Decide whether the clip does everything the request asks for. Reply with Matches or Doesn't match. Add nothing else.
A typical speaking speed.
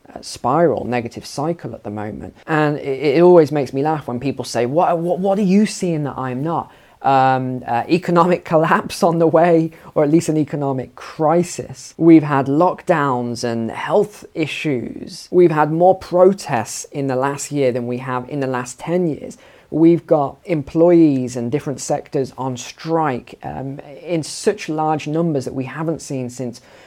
Matches